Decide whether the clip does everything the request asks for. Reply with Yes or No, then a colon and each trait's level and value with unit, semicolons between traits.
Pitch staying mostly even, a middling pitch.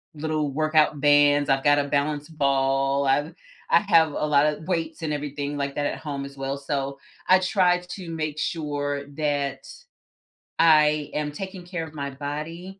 Yes: narrow, 2.1 semitones; medium, 150 Hz